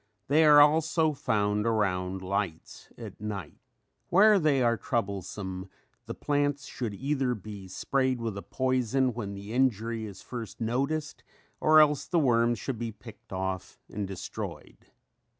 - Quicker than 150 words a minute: No, average, 145 wpm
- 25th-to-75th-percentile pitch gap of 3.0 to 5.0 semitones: No, wide, 5.4 semitones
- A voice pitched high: No, low, 115 Hz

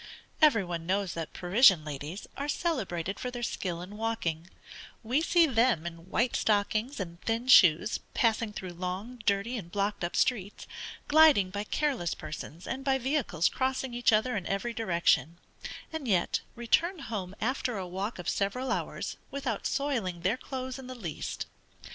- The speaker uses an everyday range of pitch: No, wide, 6.0 semitones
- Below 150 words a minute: No, average, 165 wpm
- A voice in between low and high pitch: No, high, 215 Hz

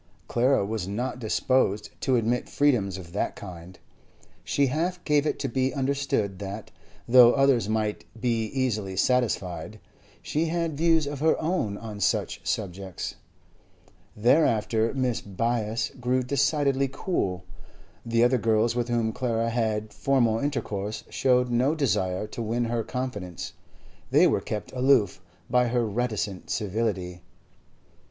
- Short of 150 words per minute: Yes, slow, 135 wpm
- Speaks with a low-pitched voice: Yes, low, 115 Hz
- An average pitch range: Yes, average, 3.8 semitones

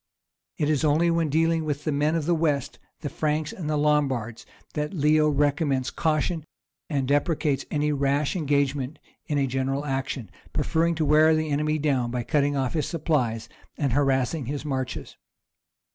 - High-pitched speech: No, medium, 145 Hz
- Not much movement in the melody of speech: Yes, narrow, 2.2 semitones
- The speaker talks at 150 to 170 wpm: Yes, average, 160 wpm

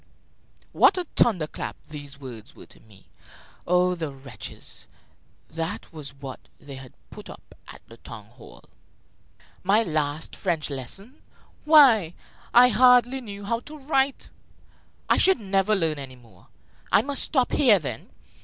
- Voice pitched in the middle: Yes, medium, 175 Hz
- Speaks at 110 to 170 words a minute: Yes, average, 145 wpm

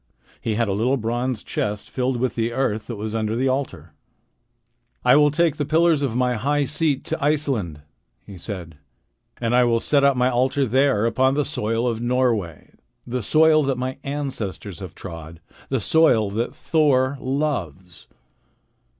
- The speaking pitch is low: Yes, low, 125 Hz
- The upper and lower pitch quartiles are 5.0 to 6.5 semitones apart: No, average, 4.5 semitones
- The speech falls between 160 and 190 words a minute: Yes, average, 170 wpm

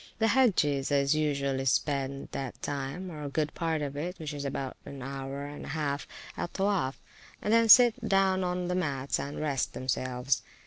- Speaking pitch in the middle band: Yes, medium, 145 Hz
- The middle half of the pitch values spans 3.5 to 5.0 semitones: Yes, average, 4.7 semitones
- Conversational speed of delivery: Yes, average, 175 wpm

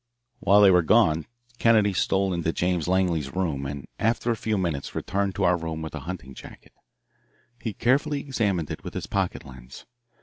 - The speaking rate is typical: Yes, average, 180 wpm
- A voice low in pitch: Yes, very low, 90 Hz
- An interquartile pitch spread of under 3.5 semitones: No, average, 4.3 semitones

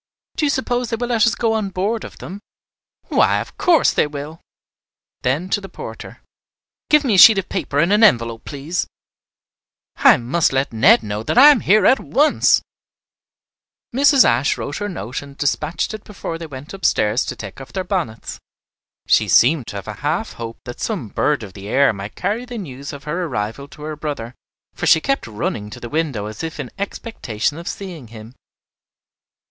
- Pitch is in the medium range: Yes, medium, 150 Hz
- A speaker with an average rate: Yes, average, 195 wpm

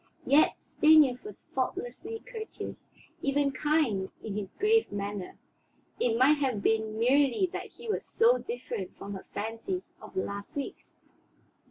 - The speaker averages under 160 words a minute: Yes, average, 145 wpm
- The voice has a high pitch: Yes, very high, 275 Hz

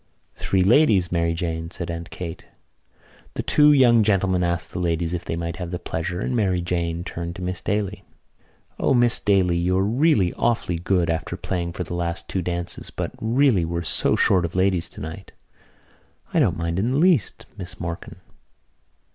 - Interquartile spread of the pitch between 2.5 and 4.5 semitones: Yes, average, 2.9 semitones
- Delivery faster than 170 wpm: Yes, average, 180 wpm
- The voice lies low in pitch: Yes, very low, 90 Hz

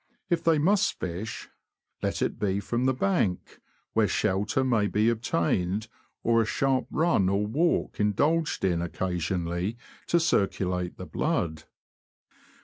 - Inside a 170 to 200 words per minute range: No, slow, 135 wpm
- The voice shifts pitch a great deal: Yes, wide, 6.2 semitones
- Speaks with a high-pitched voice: No, low, 105 Hz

